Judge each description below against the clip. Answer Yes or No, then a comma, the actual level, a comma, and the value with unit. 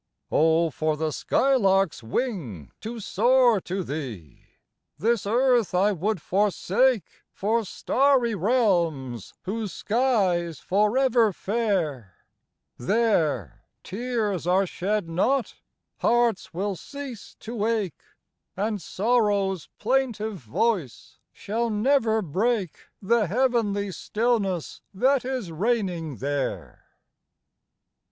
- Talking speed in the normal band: No, slow, 100 wpm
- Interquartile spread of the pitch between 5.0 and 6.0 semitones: Yes, average, 5.3 semitones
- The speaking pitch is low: No, high, 205 Hz